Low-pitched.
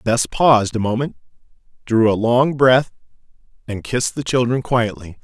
Yes: low, 120 Hz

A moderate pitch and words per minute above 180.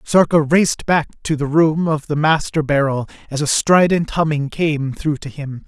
Yes: medium, 150 Hz; average, 190 wpm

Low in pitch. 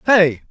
No: medium, 180 Hz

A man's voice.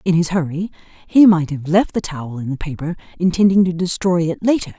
No: female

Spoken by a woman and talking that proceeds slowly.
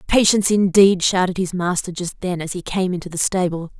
No: female; fast, 205 wpm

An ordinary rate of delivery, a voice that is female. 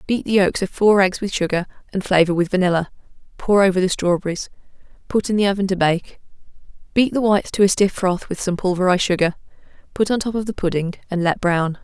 No: fast, 215 wpm; female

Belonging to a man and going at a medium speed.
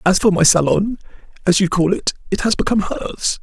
No: male; fast, 210 wpm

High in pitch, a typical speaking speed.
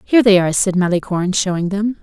No: high, 195 Hz; fast, 210 wpm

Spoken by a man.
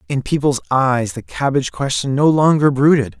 Yes: male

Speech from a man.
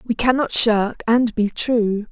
No: female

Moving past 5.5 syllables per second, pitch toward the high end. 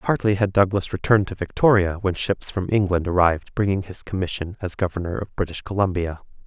No: 5.9 syllables/s; very low, 95 Hz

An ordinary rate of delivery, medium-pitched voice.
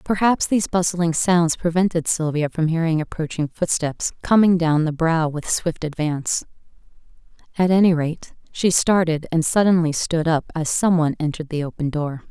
Yes: average, 160 wpm; medium, 165 Hz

